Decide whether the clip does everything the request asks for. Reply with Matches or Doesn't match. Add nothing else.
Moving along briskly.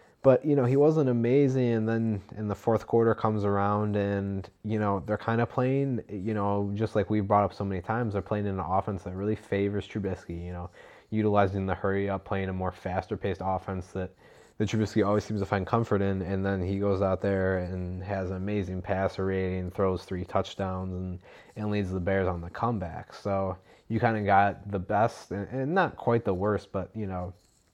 Matches